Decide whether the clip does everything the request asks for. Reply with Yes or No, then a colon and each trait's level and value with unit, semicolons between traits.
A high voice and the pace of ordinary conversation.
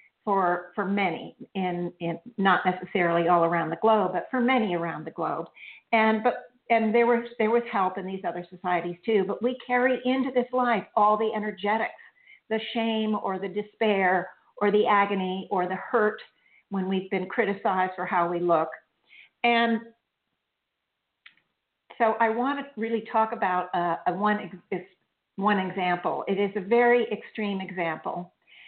Yes: high, 205 Hz; average, 160 wpm